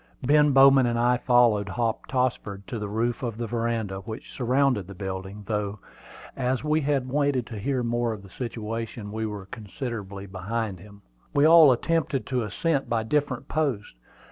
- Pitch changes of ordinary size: Yes, average, 4.2 semitones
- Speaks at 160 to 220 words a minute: Yes, average, 170 wpm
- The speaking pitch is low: Yes, low, 115 Hz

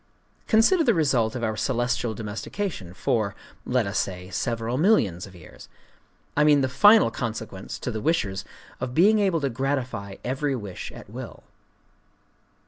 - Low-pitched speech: Yes, low, 120 Hz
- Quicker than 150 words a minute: No, average, 140 wpm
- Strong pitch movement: Yes, wide, 6.1 semitones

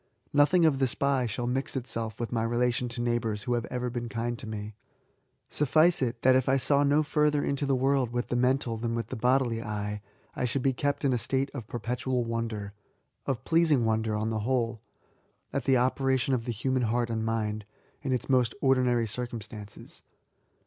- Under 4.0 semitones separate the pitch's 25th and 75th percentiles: Yes, average, 2.7 semitones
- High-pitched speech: No, low, 120 Hz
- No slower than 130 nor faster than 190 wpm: No, fast, 205 wpm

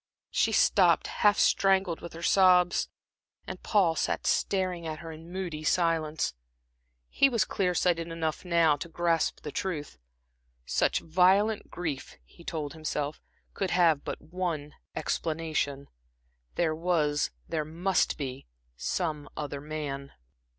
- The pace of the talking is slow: Yes, slow, 130 wpm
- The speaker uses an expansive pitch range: No, average, 2.8 semitones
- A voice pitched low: No, medium, 165 Hz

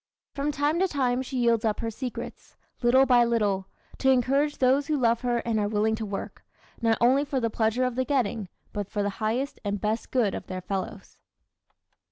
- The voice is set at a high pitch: Yes, high, 235 Hz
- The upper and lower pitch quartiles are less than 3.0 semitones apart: No, average, 3.5 semitones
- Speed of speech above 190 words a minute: Yes, fast, 205 wpm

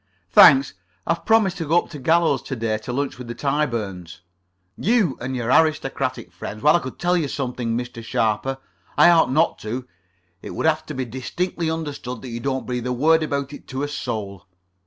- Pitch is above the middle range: No, low, 135 Hz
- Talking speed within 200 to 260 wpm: Yes, fast, 205 wpm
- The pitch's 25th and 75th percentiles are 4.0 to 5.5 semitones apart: Yes, average, 4.9 semitones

